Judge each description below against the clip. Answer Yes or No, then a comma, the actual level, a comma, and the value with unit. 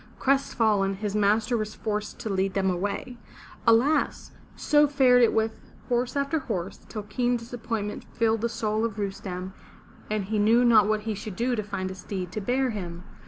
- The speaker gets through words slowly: No, average, 180 wpm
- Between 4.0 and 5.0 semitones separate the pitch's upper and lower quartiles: No, average, 3.2 semitones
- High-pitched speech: Yes, high, 215 Hz